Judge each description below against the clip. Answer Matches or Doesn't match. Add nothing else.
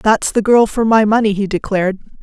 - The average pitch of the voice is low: Doesn't match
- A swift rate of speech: Matches